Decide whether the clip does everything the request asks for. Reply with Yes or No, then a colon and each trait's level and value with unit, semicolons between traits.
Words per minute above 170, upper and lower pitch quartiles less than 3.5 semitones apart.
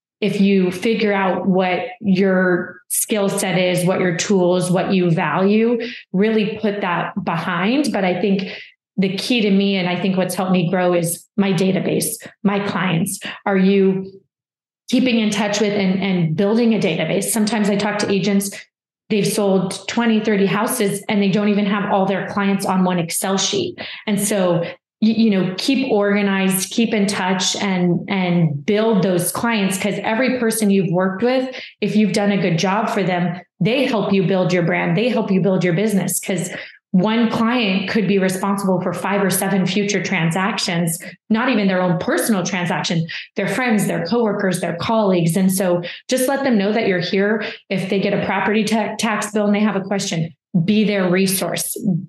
Yes: average, 185 wpm; narrow, 2.4 semitones